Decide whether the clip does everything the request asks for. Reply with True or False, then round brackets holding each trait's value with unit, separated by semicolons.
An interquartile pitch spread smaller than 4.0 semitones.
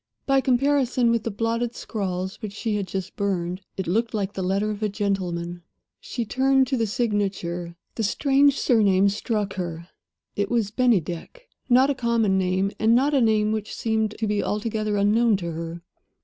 True (3.5 semitones)